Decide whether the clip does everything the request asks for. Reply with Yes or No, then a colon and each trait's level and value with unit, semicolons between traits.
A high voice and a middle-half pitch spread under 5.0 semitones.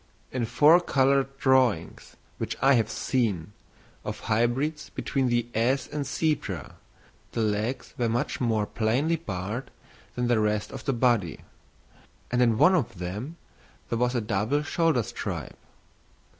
No: low, 120 Hz; average, 4.0 semitones